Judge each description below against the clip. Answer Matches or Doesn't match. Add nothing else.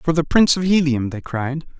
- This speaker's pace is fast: Matches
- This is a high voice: Doesn't match